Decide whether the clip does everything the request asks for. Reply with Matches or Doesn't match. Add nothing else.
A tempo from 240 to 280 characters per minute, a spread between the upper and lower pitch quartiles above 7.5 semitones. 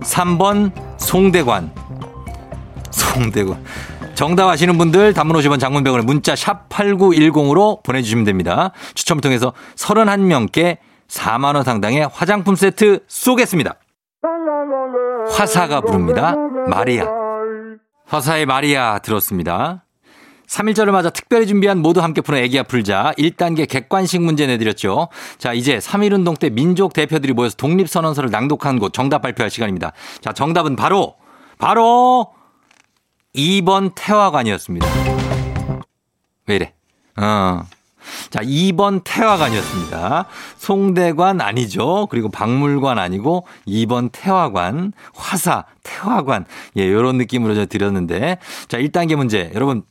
Matches